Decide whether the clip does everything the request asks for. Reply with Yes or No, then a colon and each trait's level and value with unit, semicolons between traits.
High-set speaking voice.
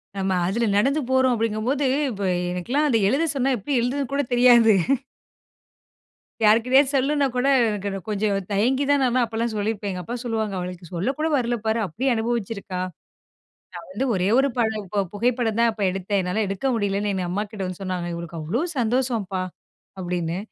Yes: high, 220 Hz